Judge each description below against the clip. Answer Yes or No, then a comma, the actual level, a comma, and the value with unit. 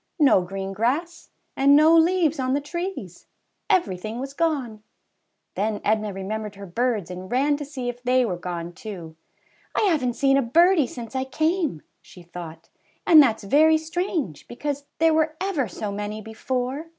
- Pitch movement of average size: No, wide, 7.0 semitones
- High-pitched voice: Yes, very high, 255 Hz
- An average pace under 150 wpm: No, average, 165 wpm